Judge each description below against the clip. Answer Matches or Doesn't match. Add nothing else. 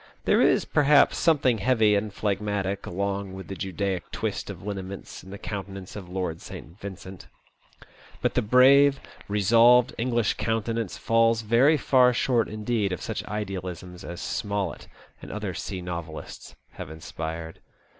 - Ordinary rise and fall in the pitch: Matches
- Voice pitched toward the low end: Matches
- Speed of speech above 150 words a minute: Doesn't match